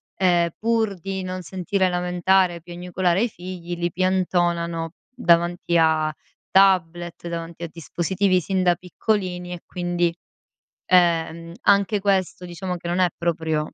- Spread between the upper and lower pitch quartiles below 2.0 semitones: Yes, narrow, 1.6 semitones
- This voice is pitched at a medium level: Yes, medium, 175 Hz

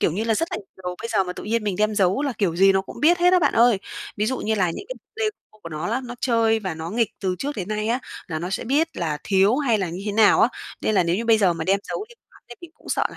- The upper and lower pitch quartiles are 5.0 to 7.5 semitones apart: No, average, 4.3 semitones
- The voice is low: No, high, 215 Hz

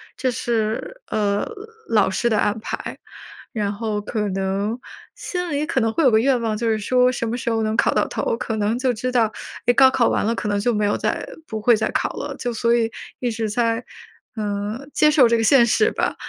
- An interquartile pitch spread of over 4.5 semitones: No, average, 2.8 semitones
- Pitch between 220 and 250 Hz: Yes, high, 230 Hz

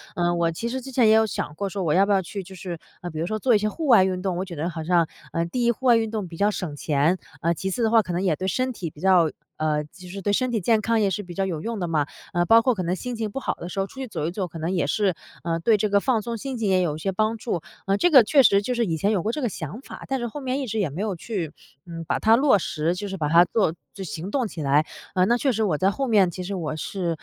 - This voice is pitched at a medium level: No, high, 195 Hz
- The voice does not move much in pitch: No, average, 4.8 semitones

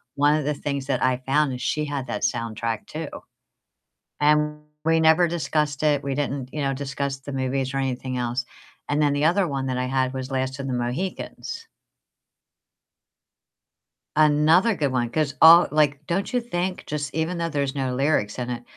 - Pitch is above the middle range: No, medium, 140 Hz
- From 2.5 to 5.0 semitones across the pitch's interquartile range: Yes, average, 2.8 semitones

